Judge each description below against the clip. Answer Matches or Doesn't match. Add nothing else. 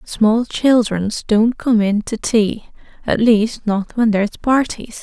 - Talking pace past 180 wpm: Doesn't match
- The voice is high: Matches